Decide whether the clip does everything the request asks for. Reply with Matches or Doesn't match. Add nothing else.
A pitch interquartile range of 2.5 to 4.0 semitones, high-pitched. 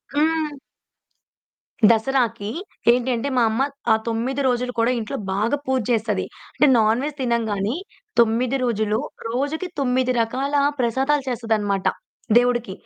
Matches